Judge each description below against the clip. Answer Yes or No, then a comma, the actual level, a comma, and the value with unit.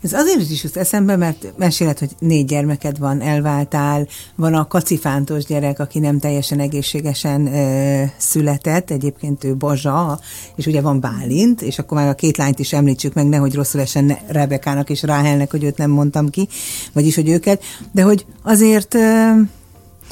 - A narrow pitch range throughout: Yes, narrow, 2.3 semitones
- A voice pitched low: No, medium, 145 Hz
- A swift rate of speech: Yes, fast, 165 wpm